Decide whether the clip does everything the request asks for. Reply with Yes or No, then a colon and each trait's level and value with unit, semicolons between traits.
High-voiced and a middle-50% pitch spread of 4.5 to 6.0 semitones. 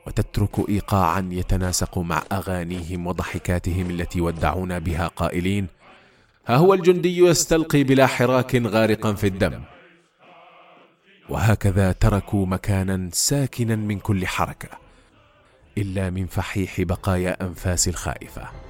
No: low, 100 Hz; average, 5.2 semitones